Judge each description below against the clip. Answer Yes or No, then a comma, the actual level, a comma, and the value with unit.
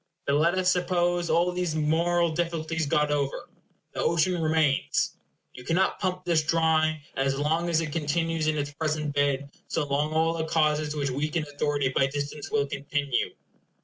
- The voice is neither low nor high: Yes, medium, 155 Hz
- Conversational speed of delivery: Yes, average, 175 wpm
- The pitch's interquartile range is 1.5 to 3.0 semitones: Yes, narrow, 2.5 semitones